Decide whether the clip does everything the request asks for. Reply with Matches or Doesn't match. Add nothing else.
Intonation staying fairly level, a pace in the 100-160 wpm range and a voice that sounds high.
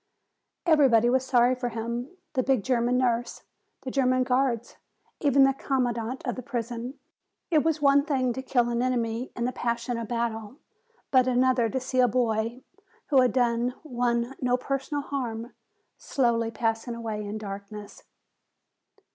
Matches